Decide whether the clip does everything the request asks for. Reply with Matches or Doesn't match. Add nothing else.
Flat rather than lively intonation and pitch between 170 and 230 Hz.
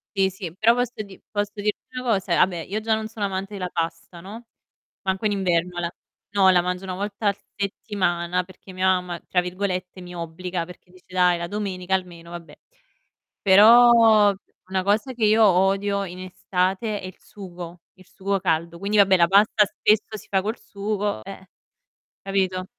Matches